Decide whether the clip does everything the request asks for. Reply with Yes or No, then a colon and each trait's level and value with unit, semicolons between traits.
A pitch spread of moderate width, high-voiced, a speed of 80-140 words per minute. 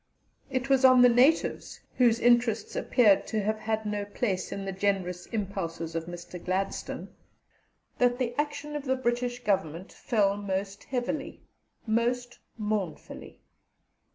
Yes: average, 4.1 semitones; high, 220 Hz; slow, 135 wpm